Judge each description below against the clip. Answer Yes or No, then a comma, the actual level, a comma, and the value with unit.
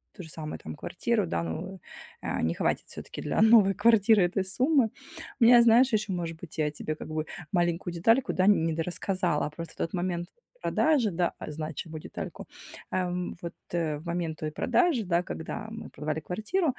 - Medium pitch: Yes, medium, 180 Hz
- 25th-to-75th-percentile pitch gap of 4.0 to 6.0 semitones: Yes, average, 5.2 semitones